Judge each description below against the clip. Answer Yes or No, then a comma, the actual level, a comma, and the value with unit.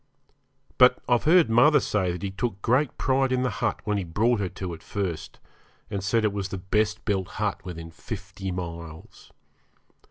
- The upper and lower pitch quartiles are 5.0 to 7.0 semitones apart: No, average, 4.5 semitones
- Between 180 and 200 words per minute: Yes, average, 185 wpm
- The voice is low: Yes, low, 100 Hz